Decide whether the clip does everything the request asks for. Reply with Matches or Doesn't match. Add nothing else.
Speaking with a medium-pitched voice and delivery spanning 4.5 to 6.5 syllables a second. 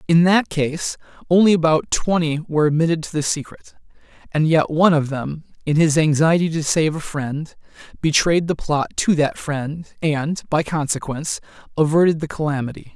Matches